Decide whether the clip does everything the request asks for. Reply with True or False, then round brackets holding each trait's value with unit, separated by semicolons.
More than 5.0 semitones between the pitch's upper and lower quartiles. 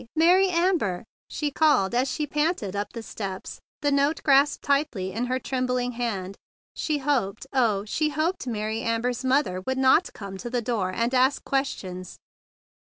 True (5.5 semitones)